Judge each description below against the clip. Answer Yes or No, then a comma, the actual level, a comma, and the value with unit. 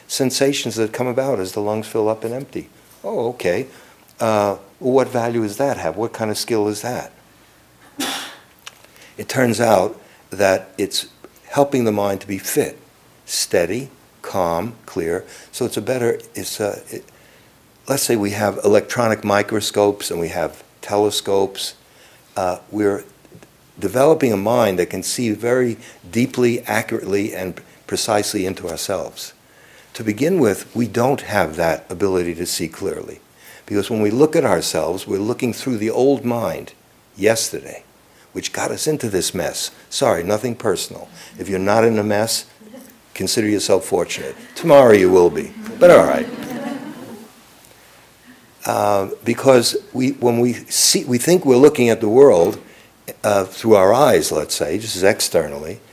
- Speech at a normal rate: Yes, average, 150 wpm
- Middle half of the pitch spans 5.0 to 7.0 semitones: No, average, 4.4 semitones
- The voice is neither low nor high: No, low, 115 Hz